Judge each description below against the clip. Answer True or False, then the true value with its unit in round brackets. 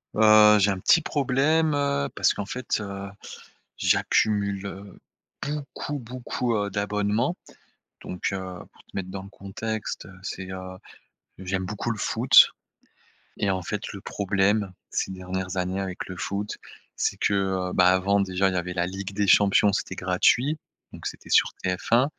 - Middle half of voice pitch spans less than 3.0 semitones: True (2.6 semitones)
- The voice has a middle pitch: False (100 Hz)